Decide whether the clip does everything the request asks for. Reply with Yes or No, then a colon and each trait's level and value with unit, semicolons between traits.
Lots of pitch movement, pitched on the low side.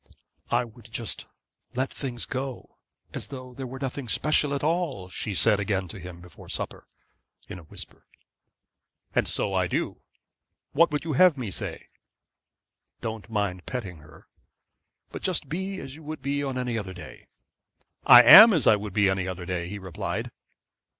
Yes: wide, 6.6 semitones; low, 120 Hz